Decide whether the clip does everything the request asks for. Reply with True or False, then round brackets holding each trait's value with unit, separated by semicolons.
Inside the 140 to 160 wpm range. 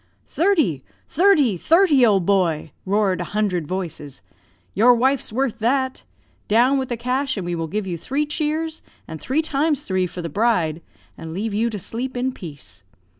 False (175 wpm)